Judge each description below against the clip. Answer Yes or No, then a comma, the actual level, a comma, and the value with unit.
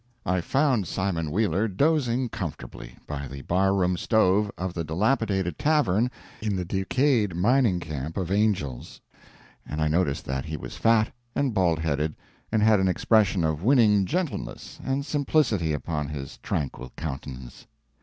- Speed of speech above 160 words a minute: No, average, 150 wpm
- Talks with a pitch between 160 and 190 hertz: No, very low, 95 Hz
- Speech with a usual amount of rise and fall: No, wide, 6.1 semitones